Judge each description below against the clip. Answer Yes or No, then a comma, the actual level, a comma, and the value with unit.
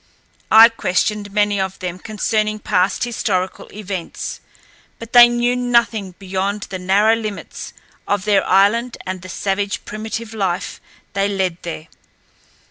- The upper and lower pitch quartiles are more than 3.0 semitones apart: No, average, 2.7 semitones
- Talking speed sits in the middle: No, slow, 130 wpm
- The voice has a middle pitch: No, high, 205 Hz